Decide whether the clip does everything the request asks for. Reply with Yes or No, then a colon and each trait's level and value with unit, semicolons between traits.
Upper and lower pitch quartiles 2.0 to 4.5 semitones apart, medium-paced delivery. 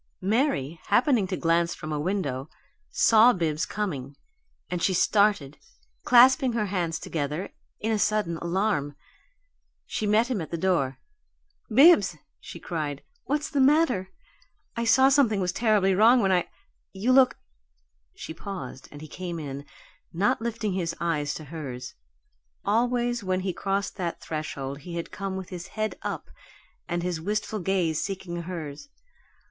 No: average, 5.1 semitones; average, 155 wpm